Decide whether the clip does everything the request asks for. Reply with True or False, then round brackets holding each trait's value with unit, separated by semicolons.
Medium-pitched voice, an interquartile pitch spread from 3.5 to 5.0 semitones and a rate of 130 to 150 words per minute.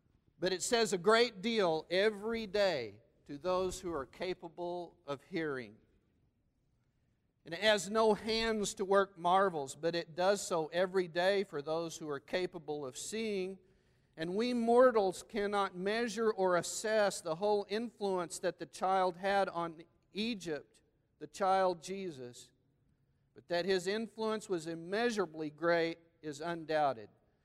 True (180 Hz; 4.4 semitones; 140 wpm)